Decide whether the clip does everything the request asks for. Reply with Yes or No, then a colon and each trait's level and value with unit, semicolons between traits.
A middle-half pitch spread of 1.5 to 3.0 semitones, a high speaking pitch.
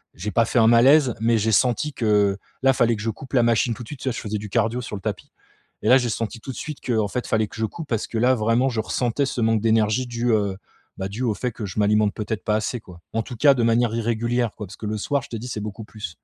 No: narrow, 2.4 semitones; low, 115 Hz